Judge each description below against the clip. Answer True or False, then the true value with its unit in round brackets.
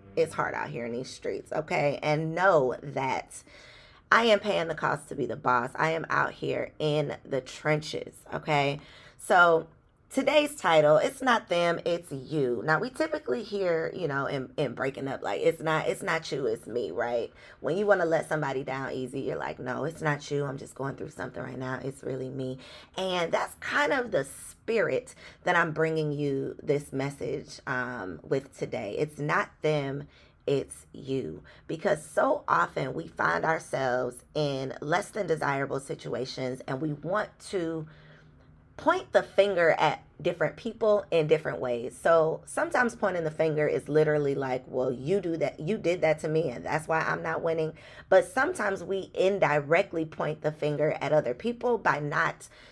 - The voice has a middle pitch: True (155 Hz)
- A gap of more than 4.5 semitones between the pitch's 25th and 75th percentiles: True (4.9 semitones)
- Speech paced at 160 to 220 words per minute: True (180 wpm)